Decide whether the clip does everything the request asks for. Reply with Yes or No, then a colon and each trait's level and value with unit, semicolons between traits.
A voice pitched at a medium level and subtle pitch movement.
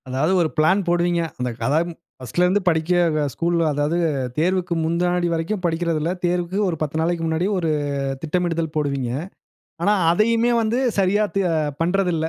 Yes: medium, 170 Hz; narrow, 2.1 semitones